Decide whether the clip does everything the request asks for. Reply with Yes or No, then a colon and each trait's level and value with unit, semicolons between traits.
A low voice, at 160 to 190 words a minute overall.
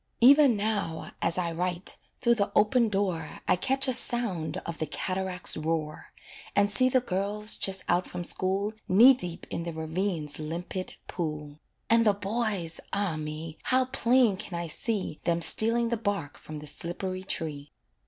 No: medium, 185 Hz; average, 165 wpm